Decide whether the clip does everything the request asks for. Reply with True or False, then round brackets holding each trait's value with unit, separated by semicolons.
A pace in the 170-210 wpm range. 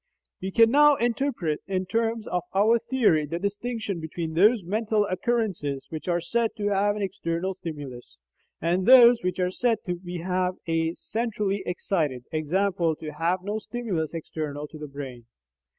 False (155 wpm)